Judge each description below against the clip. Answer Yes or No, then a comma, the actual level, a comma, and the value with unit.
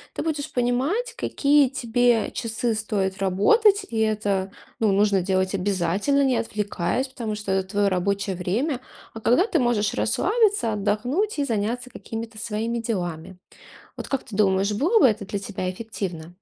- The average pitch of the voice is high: Yes, high, 215 Hz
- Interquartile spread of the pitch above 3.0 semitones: Yes, average, 4.4 semitones